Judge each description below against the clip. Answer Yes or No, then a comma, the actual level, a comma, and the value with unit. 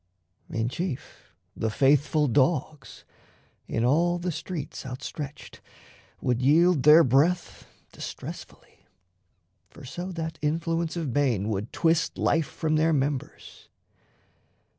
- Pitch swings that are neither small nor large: Yes, average, 3.9 semitones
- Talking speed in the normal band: No, slow, 110 wpm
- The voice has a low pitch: No, medium, 150 Hz